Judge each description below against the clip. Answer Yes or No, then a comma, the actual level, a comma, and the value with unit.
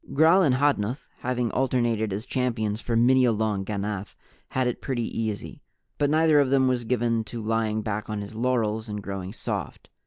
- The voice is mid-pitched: No, low, 115 Hz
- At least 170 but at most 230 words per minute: Yes, average, 185 wpm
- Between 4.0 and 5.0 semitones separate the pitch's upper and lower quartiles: No, average, 3.2 semitones